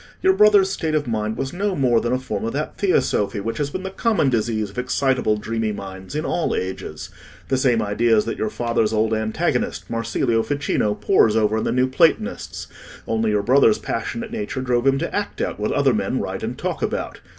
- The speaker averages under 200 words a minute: No, fast, 205 wpm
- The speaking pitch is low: Yes, low, 115 Hz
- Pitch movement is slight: No, average, 4.4 semitones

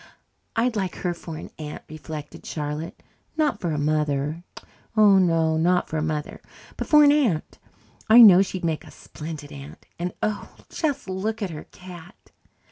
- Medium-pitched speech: Yes, medium, 170 Hz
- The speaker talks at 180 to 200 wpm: No, average, 170 wpm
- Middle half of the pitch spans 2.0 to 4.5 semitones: No, average, 4.9 semitones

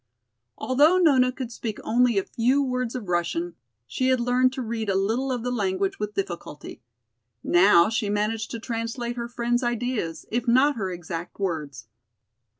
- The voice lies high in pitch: Yes, high, 230 Hz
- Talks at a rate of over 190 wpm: No, average, 165 wpm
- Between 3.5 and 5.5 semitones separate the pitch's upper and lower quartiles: Yes, average, 4.3 semitones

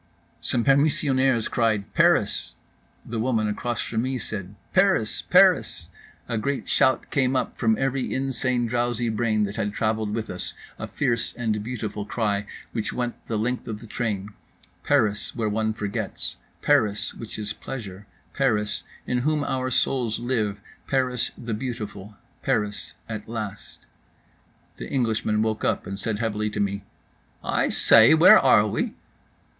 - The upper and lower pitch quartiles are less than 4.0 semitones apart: Yes, average, 2.9 semitones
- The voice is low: Yes, low, 110 Hz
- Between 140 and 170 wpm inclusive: Yes, average, 145 wpm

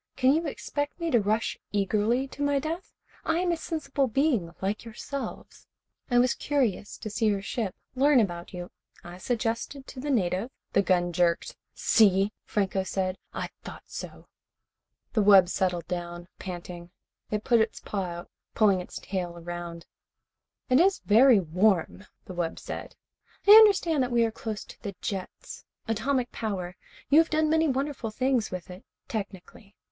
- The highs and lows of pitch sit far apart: Yes, wide, 6.5 semitones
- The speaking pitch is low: No, high, 215 Hz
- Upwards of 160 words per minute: Yes, average, 170 wpm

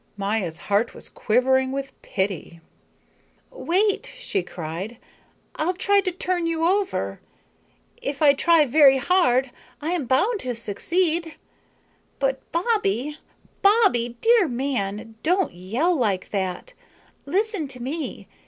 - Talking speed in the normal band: No, slow, 120 wpm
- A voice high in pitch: Yes, very high, 280 Hz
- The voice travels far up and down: Yes, wide, 7.6 semitones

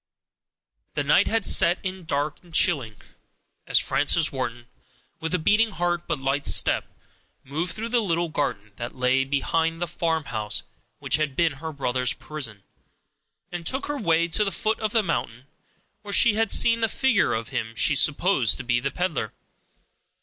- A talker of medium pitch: Yes, medium, 160 Hz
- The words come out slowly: No, average, 170 wpm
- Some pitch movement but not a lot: No, wide, 6.1 semitones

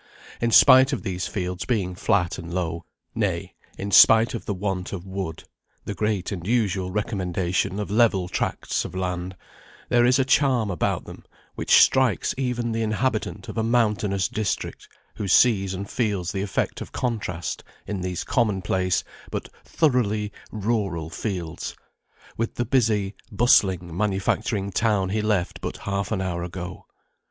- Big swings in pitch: No, average, 3.6 semitones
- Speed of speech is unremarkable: Yes, average, 155 wpm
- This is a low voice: Yes, low, 100 Hz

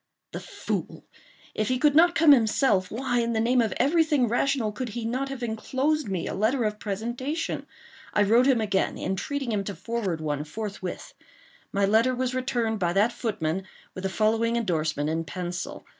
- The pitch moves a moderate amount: Yes, average, 4.8 semitones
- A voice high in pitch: Yes, high, 225 Hz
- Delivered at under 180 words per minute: No, average, 185 wpm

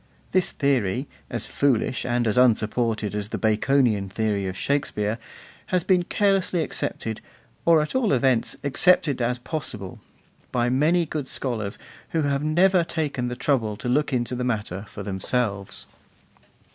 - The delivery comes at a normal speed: Yes, average, 145 wpm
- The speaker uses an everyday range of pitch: No, wide, 5.7 semitones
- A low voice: Yes, low, 125 Hz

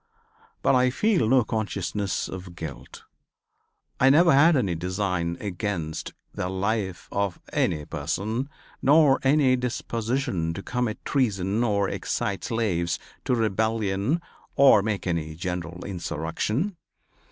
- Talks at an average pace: No, slow, 120 wpm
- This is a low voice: Yes, low, 105 Hz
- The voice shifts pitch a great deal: Yes, wide, 5.8 semitones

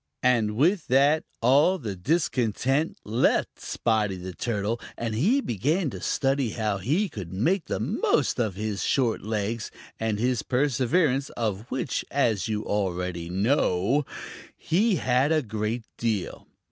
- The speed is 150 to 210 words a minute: No, average, 140 wpm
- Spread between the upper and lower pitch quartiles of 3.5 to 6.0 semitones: Yes, average, 5.0 semitones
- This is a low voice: Yes, low, 115 Hz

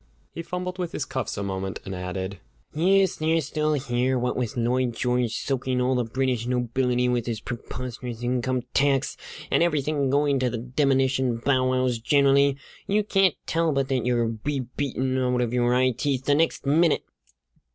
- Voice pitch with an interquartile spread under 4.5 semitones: Yes, average, 2.8 semitones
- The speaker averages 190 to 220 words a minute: No, average, 175 wpm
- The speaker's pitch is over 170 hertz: No, low, 130 Hz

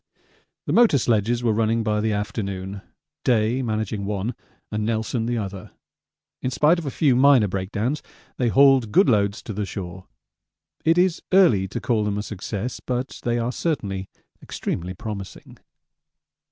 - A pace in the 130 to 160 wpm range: Yes, average, 155 wpm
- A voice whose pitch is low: Yes, low, 110 Hz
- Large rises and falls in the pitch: No, average, 3.8 semitones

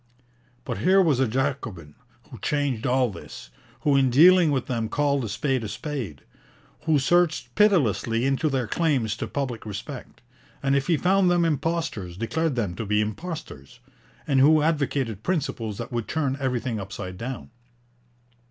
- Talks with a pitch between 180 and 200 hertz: No, low, 135 Hz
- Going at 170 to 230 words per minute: No, average, 160 wpm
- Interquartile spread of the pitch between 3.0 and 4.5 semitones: No, wide, 5.5 semitones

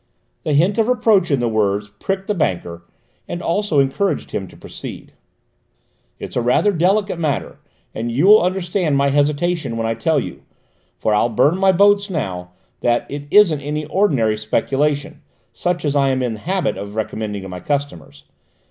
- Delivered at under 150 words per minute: No, average, 175 wpm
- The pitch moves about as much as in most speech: No, wide, 8.1 semitones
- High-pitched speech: No, medium, 145 Hz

